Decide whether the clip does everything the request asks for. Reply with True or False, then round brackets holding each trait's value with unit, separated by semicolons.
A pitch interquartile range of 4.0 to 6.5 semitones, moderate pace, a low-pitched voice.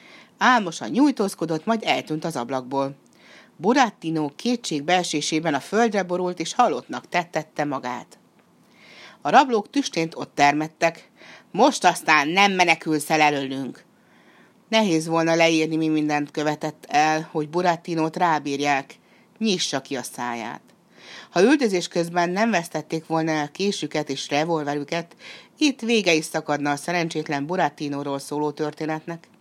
False (4.7 semitones; 120 wpm; 165 Hz)